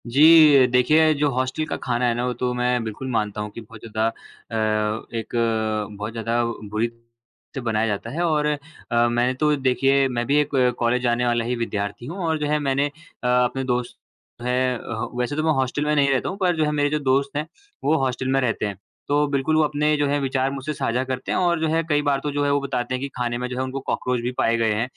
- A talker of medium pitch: No, low, 130 Hz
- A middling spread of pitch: Yes, average, 3.4 semitones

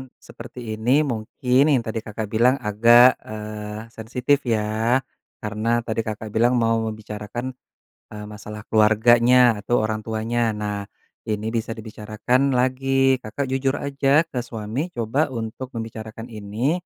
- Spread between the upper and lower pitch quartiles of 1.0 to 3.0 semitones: Yes, average, 2.7 semitones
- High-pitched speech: No, low, 115 Hz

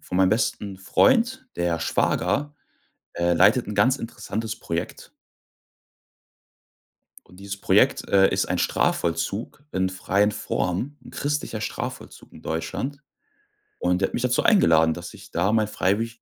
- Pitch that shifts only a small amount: No, average, 4.9 semitones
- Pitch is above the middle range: No, low, 100 Hz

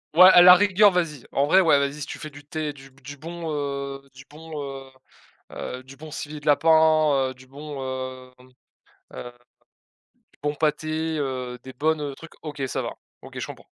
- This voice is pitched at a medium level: Yes, medium, 145 Hz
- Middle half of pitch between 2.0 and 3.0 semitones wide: Yes, narrow, 2.5 semitones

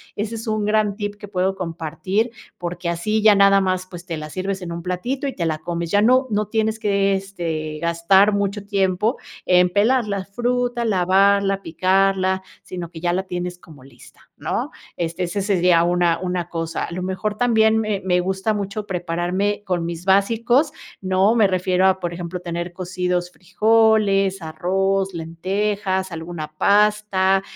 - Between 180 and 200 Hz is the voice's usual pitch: Yes, high, 190 Hz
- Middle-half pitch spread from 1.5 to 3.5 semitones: Yes, average, 2.7 semitones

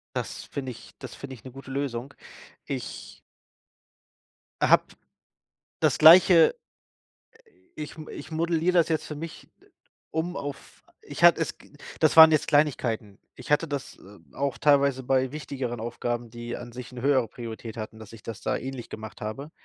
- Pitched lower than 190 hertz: Yes, low, 135 Hz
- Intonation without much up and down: No, average, 4.3 semitones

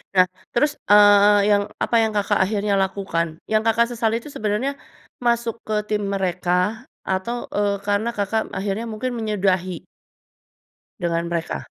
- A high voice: Yes, high, 205 Hz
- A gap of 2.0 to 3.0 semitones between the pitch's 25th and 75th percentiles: Yes, average, 2.7 semitones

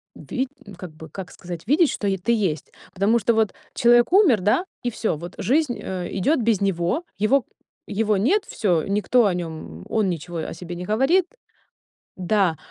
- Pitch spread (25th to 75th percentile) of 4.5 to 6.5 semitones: Yes, average, 5.2 semitones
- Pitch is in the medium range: No, high, 205 Hz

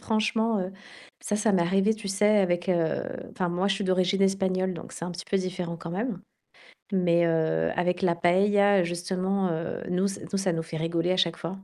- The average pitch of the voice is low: No, medium, 185 Hz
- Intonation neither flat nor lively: No, narrow, 2.3 semitones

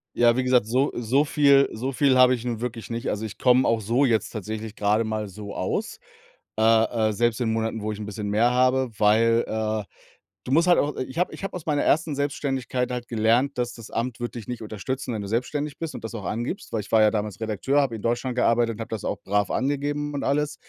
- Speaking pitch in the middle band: No, low, 120 Hz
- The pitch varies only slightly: No, average, 3.3 semitones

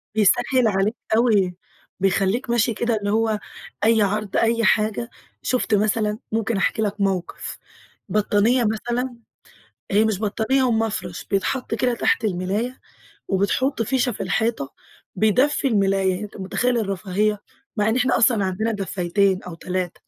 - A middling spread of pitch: Yes, average, 3.0 semitones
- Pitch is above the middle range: Yes, high, 215 Hz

